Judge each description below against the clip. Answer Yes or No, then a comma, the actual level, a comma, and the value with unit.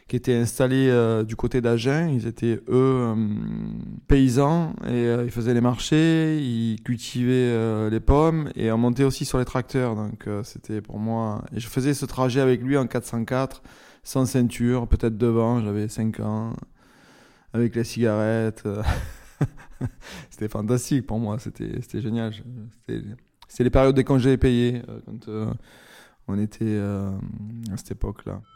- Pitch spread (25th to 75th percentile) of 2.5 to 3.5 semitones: Yes, average, 2.9 semitones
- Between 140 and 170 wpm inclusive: Yes, average, 160 wpm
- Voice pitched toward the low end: Yes, low, 120 Hz